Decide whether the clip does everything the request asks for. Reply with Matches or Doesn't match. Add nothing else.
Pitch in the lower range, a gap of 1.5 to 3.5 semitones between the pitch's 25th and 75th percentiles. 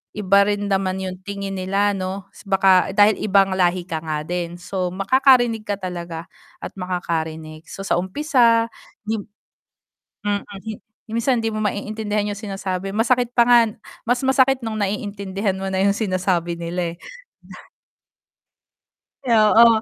Doesn't match